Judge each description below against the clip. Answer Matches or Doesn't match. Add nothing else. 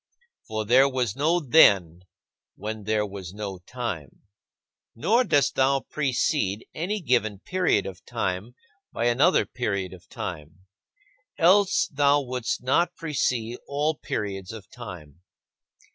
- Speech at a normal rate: Doesn't match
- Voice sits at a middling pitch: Doesn't match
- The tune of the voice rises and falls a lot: Matches